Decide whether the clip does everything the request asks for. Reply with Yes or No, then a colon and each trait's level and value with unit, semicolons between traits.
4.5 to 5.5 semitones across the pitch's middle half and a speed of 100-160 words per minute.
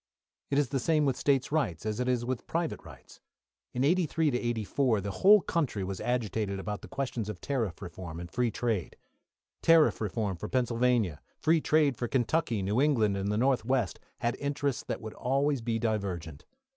No: average, 5.1 semitones; average, 185 wpm